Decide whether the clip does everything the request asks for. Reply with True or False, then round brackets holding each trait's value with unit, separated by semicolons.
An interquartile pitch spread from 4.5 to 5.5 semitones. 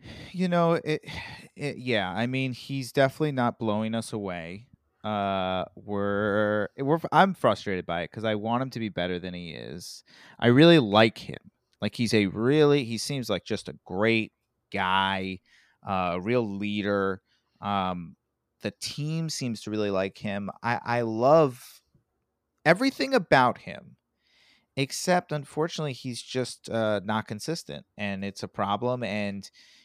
True (5.2 semitones)